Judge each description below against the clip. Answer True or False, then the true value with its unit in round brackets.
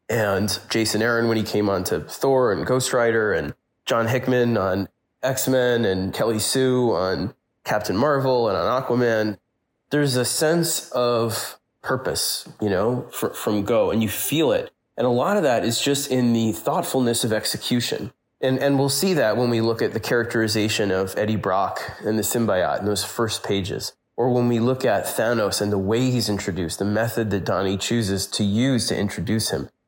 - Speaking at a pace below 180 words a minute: False (190 wpm)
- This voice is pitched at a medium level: False (115 Hz)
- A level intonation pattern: False (3.2 semitones)